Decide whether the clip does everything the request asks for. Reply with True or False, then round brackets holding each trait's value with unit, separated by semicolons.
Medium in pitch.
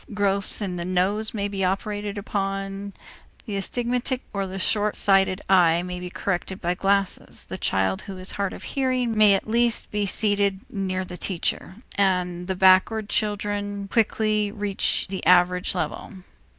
False (195 Hz)